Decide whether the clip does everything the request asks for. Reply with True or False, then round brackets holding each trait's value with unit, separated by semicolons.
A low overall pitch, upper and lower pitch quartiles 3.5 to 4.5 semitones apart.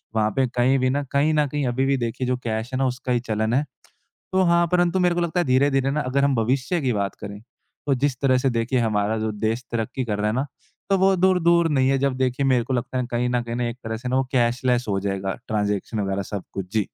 True (125 Hz; 3.8 semitones)